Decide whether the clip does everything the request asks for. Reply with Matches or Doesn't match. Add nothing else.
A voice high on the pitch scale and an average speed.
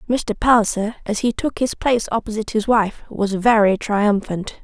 Matches